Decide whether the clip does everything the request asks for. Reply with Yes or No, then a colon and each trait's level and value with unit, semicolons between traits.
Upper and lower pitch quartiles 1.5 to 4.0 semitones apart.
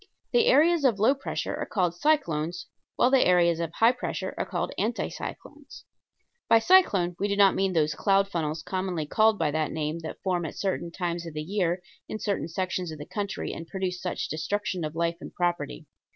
Yes: average, 3.7 semitones